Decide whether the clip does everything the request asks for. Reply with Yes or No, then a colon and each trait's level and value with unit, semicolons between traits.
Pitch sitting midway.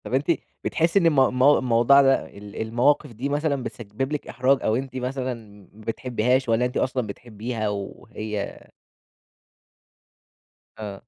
No: low, 125 Hz